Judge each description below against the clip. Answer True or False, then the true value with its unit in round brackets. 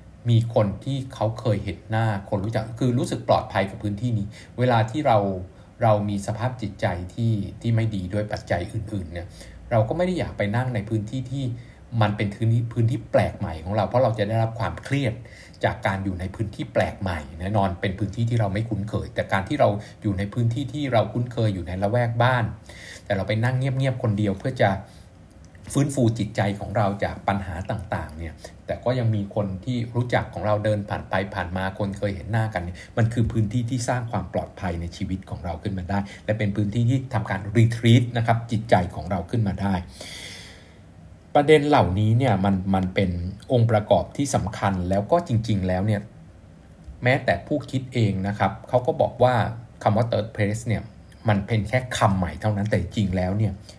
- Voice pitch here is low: True (105 Hz)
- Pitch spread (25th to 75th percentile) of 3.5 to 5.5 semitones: False (3.1 semitones)